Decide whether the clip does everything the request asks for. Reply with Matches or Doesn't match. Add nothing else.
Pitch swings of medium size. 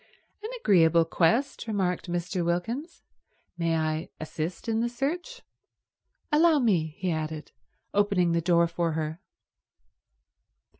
Doesn't match